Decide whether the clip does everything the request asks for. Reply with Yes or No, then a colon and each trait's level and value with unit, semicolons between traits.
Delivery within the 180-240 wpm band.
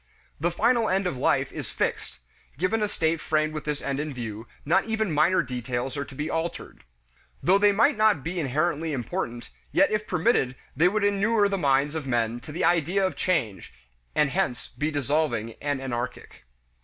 Yes: average, 185 wpm